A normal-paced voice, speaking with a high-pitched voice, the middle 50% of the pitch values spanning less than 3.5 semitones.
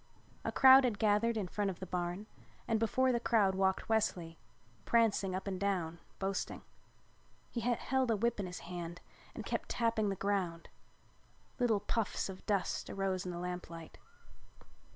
No: average, 160 wpm; high, 200 Hz; average, 3.9 semitones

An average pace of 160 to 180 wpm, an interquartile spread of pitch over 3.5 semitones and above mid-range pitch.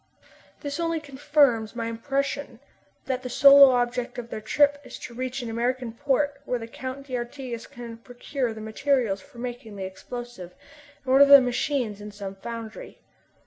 No: average, 165 wpm; average, 3.2 semitones; high, 245 Hz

